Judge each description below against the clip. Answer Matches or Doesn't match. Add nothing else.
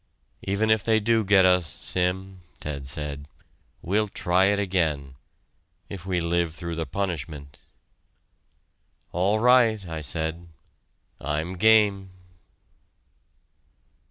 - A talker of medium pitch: Doesn't match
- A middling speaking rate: Doesn't match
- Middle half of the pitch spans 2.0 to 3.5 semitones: Doesn't match